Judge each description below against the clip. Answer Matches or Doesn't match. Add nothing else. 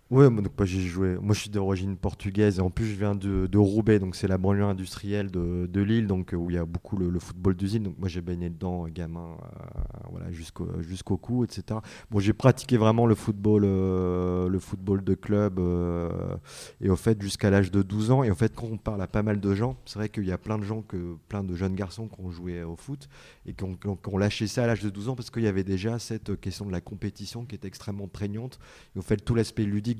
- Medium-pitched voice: Doesn't match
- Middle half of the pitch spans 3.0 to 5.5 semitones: Doesn't match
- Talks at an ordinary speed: Doesn't match